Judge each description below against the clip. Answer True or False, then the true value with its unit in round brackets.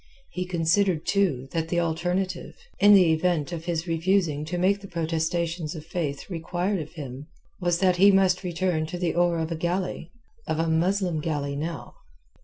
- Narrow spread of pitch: True (2.3 semitones)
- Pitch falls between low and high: True (170 Hz)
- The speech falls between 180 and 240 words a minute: False (170 wpm)